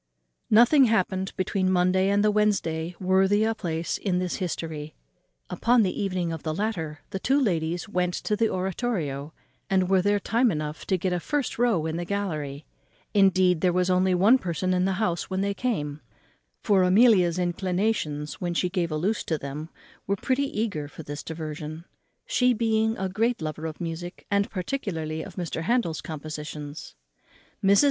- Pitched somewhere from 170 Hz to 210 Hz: Yes, medium, 185 Hz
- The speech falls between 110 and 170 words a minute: No, average, 180 wpm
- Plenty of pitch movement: No, average, 4.2 semitones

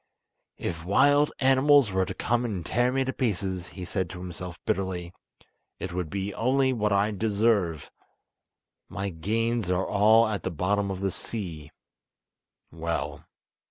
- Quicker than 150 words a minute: No, average, 145 wpm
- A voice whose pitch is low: Yes, low, 100 Hz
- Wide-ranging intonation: No, average, 4.1 semitones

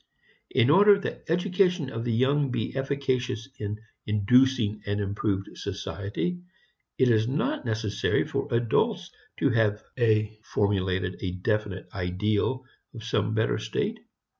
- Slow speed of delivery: Yes, slow, 125 wpm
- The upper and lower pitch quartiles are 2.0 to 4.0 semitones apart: No, average, 4.4 semitones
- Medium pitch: No, low, 115 Hz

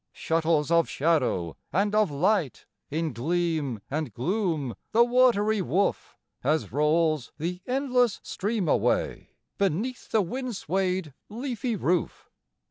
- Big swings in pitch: Yes, wide, 5.8 semitones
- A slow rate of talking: Yes, slow, 120 wpm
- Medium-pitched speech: Yes, medium, 175 Hz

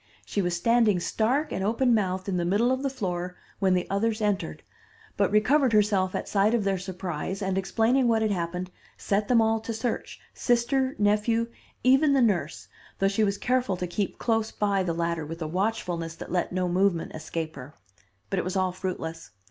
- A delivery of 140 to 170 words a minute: No, average, 195 wpm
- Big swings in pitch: No, average, 4.0 semitones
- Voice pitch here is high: Yes, high, 200 Hz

